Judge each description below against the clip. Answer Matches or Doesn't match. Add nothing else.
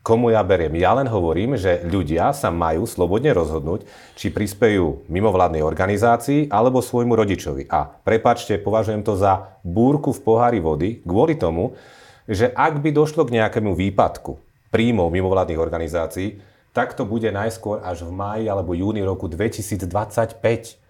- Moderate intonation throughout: Matches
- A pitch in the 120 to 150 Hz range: Doesn't match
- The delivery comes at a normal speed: Matches